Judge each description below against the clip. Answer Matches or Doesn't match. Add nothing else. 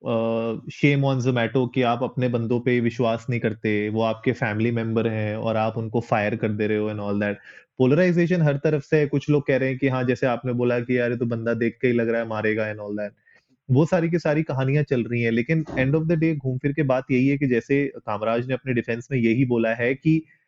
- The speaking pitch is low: Matches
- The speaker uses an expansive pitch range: Doesn't match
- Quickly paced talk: Matches